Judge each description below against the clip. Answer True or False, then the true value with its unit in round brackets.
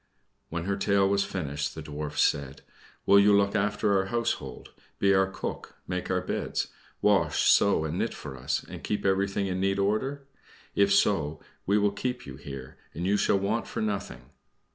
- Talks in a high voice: False (95 Hz)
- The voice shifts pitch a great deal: False (4.3 semitones)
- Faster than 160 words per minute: True (185 wpm)